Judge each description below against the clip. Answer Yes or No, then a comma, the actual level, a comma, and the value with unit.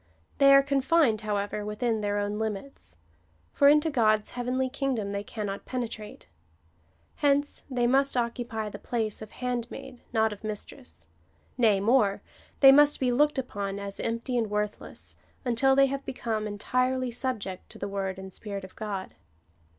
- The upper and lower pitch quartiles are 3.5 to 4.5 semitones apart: Yes, average, 4.1 semitones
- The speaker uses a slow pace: No, average, 160 wpm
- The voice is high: Yes, high, 230 Hz